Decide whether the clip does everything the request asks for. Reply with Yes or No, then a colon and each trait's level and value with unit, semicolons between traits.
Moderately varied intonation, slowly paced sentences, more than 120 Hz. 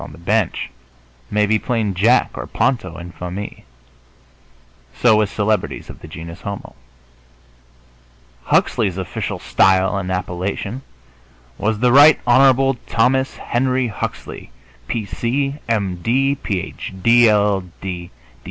No: average, 4.4 semitones; slow, 120 wpm; low, 110 Hz